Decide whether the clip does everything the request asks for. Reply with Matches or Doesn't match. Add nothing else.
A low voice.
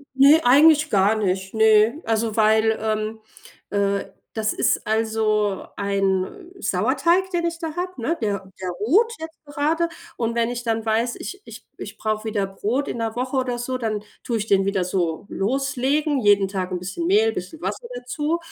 Doesn't match